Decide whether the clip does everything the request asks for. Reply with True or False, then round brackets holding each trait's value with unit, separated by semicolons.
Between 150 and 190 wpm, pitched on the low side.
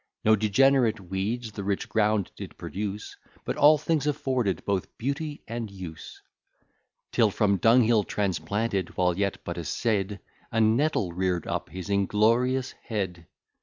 False (140 wpm; 105 Hz)